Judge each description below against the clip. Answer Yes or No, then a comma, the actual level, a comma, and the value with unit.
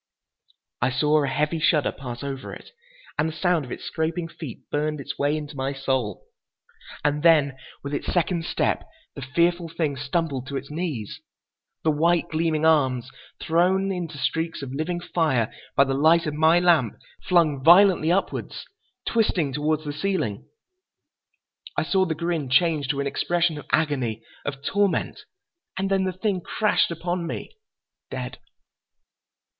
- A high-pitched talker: No, medium, 155 Hz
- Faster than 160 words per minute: No, average, 155 wpm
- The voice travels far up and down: No, average, 3.7 semitones